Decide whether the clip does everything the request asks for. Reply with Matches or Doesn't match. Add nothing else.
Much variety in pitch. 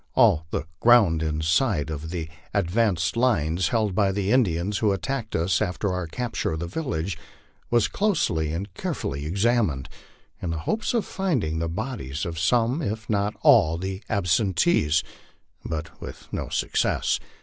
Matches